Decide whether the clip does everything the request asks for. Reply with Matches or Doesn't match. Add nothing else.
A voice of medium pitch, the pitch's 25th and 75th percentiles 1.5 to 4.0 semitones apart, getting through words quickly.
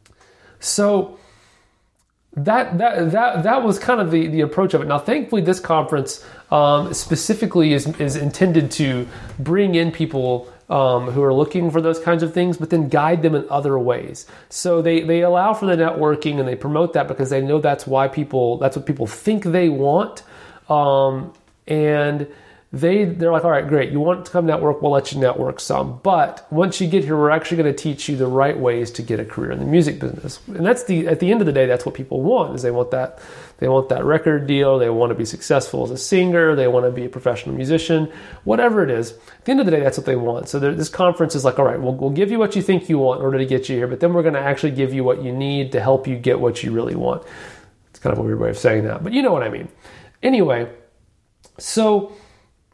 Doesn't match